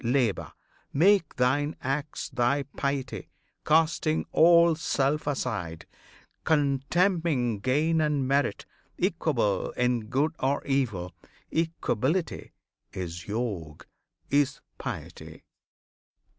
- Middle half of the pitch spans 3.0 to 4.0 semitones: No, average, 4.4 semitones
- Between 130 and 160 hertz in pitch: Yes, medium, 140 Hz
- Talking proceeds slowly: Yes, slow, 90 wpm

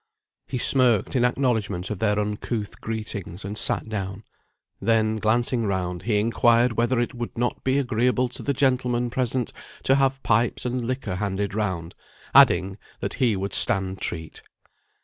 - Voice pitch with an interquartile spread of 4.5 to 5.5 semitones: No, average, 3.5 semitones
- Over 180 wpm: No, average, 155 wpm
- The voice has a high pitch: No, low, 115 Hz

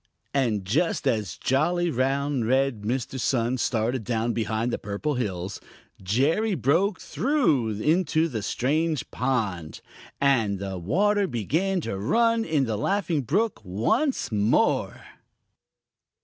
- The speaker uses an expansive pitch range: Yes, wide, 7.0 semitones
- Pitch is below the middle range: Yes, low, 130 Hz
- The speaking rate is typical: No, slow, 120 wpm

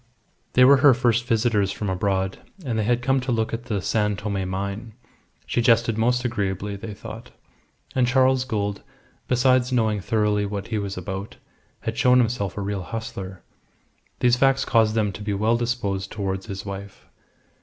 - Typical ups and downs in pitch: Yes, average, 3.4 semitones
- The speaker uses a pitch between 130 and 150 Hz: No, low, 110 Hz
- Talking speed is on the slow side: No, average, 175 wpm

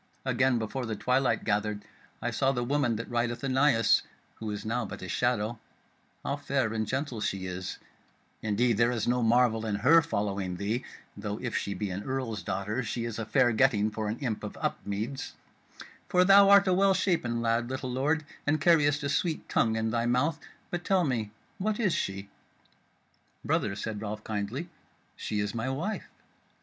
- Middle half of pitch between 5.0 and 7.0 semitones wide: No, average, 4.3 semitones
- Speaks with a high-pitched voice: No, low, 120 Hz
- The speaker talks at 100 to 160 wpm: No, average, 185 wpm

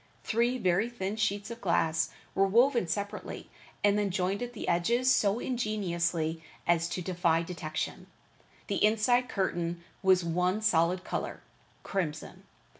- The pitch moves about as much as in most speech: Yes, average, 4.1 semitones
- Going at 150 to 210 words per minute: No, slow, 135 wpm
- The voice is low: No, high, 190 Hz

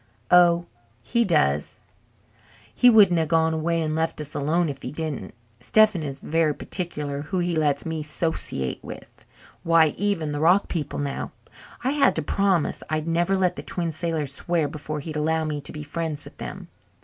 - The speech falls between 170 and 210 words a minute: Yes, average, 180 wpm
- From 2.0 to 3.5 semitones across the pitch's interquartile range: Yes, narrow, 2.6 semitones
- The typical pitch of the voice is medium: Yes, medium, 160 Hz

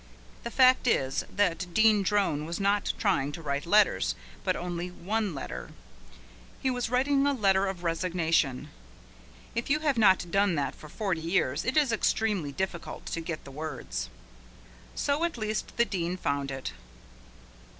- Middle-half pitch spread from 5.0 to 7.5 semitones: Yes, wide, 5.4 semitones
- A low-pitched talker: No, high, 190 Hz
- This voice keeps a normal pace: Yes, average, 160 wpm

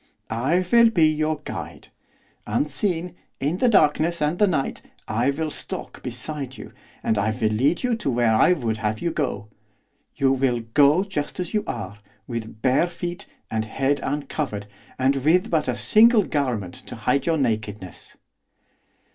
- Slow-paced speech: No, average, 160 wpm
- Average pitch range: No, wide, 6.5 semitones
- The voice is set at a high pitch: No, medium, 140 Hz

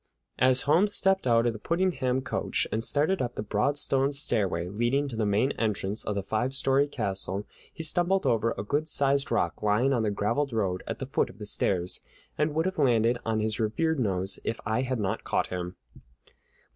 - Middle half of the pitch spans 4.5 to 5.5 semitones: Yes, average, 5.2 semitones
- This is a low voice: Yes, low, 120 Hz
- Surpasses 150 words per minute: Yes, fast, 205 wpm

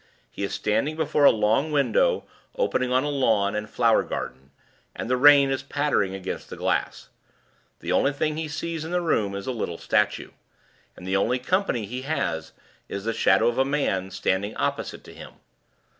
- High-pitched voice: No, low, 125 Hz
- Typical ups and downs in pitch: No, wide, 6.7 semitones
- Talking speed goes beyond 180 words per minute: Yes, average, 190 wpm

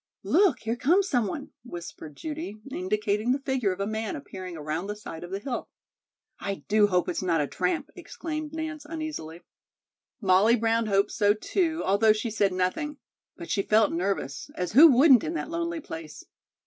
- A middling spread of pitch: No, wide, 7.9 semitones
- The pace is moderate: Yes, average, 180 wpm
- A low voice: No, high, 215 Hz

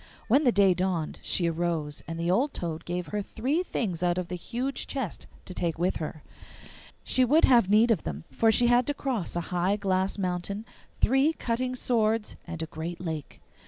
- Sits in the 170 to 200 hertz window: Yes, high, 190 Hz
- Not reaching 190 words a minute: No, average, 195 wpm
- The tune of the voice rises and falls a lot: Yes, wide, 5.8 semitones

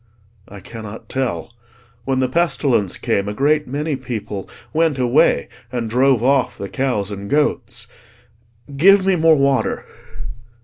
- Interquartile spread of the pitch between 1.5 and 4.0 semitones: No, average, 4.8 semitones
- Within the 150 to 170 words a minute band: No, slow, 135 wpm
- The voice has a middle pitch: No, low, 130 Hz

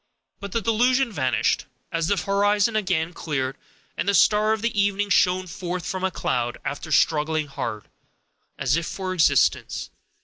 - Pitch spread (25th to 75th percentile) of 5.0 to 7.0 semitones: No, average, 4.5 semitones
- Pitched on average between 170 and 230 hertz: Yes, medium, 185 Hz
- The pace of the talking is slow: No, average, 150 wpm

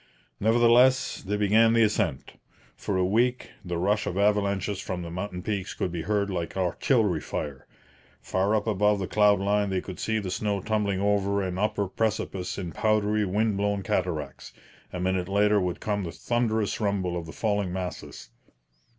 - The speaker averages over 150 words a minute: Yes, average, 175 wpm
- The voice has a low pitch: Yes, low, 100 Hz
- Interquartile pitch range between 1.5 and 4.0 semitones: Yes, narrow, 2.5 semitones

